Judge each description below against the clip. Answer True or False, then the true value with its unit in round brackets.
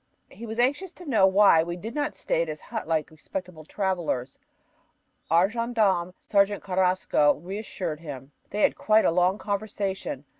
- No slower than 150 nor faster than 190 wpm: True (160 wpm)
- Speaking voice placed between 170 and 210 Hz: True (190 Hz)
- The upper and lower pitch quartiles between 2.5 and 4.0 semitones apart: False (4.4 semitones)